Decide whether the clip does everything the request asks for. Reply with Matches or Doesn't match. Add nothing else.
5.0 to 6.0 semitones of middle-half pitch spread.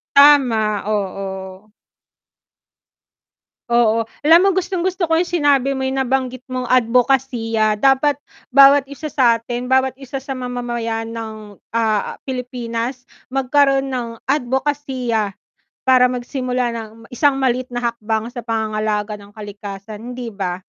Doesn't match